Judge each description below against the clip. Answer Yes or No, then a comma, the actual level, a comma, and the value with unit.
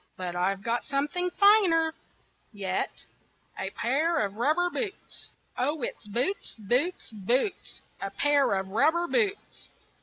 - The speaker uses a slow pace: Yes, slow, 125 wpm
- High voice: Yes, very high, 275 Hz